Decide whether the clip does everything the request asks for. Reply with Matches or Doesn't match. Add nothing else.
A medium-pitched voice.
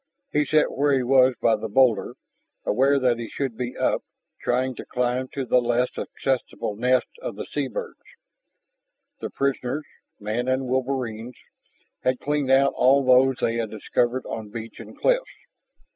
Doesn't match